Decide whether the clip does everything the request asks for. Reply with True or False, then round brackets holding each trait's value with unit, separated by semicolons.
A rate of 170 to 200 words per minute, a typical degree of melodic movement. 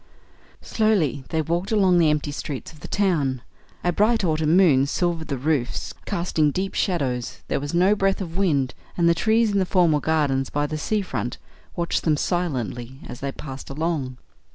True (180 wpm; 4.7 semitones)